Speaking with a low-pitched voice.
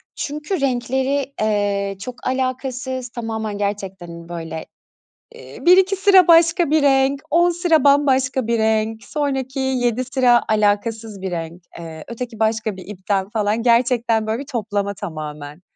No: high, 235 Hz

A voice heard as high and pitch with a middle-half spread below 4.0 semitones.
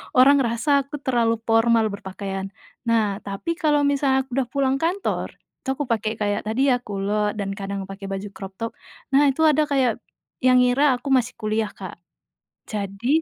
No: high, 230 Hz; average, 4.7 semitones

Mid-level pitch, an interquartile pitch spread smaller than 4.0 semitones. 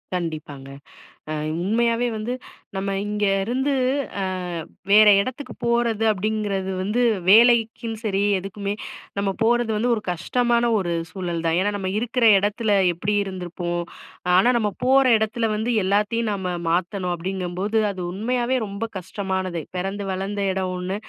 No: high, 205 Hz; average, 3.5 semitones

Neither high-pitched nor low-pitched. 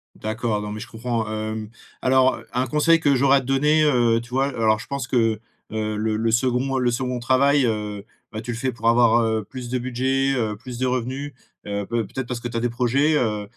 No: low, 120 Hz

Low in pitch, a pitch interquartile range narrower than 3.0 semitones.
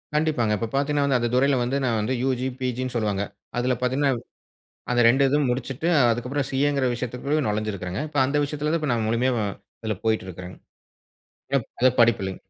No: low, 125 Hz; average, 3.5 semitones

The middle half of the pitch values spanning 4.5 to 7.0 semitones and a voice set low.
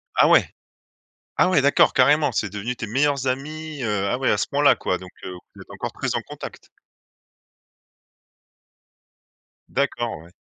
Yes: wide, 5.6 semitones; low, 130 Hz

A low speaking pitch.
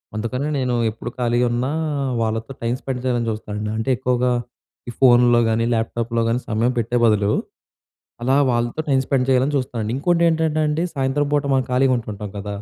Yes: low, 120 Hz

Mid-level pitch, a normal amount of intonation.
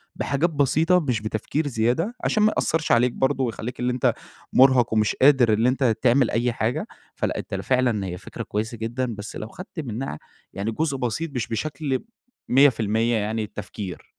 No: low, 125 Hz; average, 3.9 semitones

